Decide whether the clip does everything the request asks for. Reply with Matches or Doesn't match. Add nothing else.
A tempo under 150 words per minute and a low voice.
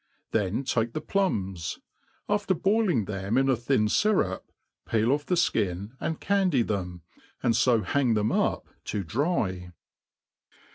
Matches